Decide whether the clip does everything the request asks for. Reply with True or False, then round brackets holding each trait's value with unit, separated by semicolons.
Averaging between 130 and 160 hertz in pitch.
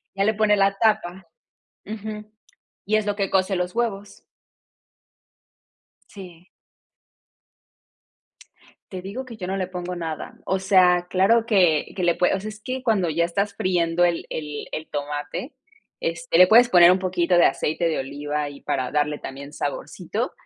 False (185 Hz)